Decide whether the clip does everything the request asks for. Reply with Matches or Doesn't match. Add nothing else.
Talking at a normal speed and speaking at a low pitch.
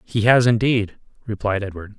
Matches